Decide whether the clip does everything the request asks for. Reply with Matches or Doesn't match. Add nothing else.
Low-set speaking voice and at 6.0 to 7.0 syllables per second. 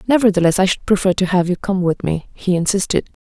Doesn't match